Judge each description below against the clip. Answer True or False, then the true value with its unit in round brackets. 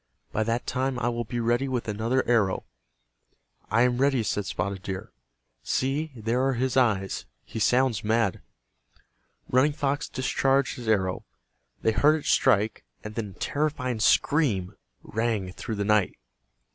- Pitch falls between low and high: False (120 Hz)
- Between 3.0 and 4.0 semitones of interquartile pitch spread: True (3.7 semitones)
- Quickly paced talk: False (150 wpm)